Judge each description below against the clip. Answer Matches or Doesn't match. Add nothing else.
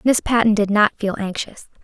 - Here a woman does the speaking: Matches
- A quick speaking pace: Doesn't match